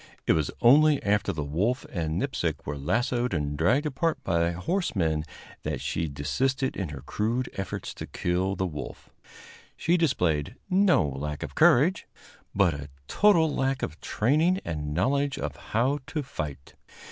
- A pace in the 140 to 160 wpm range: Yes, average, 155 wpm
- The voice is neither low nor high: No, low, 100 Hz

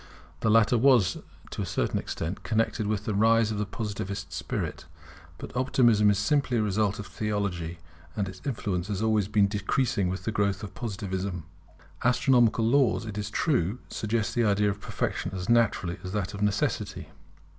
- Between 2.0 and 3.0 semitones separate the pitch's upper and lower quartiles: Yes, narrow, 2.4 semitones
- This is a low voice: Yes, low, 105 Hz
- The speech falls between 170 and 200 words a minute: Yes, average, 175 wpm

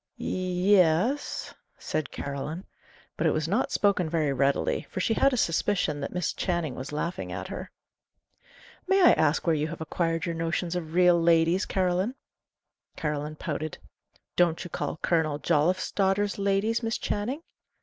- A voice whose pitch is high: No, medium, 170 Hz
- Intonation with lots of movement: No, average, 3.6 semitones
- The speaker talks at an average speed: Yes, average, 160 wpm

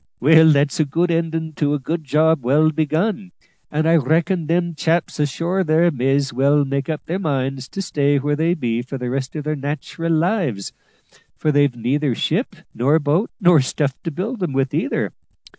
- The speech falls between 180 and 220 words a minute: Yes, average, 190 wpm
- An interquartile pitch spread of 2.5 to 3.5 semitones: Yes, average, 3.2 semitones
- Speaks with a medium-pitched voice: Yes, medium, 150 Hz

